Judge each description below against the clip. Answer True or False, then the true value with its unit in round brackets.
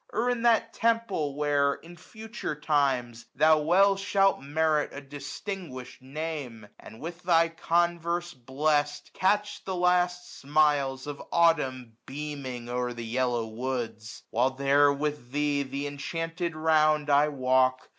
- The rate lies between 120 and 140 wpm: True (135 wpm)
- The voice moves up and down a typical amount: True (4.4 semitones)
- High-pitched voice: False (150 Hz)